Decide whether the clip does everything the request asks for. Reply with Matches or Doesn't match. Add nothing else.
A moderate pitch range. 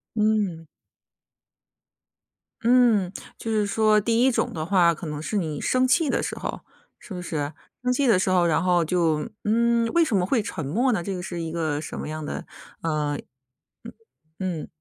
Doesn't match